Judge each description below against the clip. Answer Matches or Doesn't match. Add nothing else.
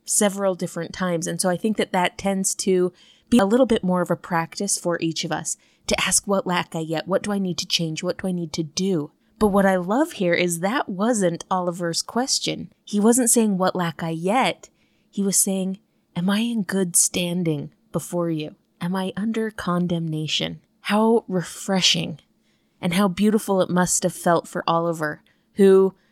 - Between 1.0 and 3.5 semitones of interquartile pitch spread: Matches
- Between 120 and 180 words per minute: Doesn't match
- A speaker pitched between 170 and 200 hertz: Matches